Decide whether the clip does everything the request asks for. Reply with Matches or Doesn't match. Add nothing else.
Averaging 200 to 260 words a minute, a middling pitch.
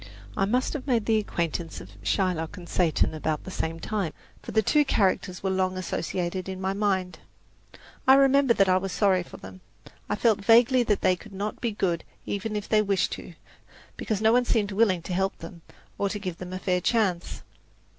Doesn't match